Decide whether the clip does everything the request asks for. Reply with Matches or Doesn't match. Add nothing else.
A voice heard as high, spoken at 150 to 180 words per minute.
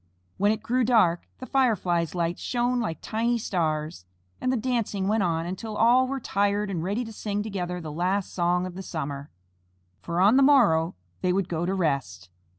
Doesn't match